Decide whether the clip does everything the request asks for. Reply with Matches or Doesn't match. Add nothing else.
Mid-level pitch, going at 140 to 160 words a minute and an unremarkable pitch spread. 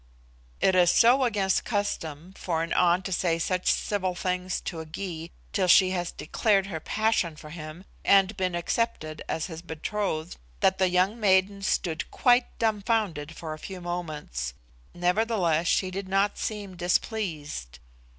Matches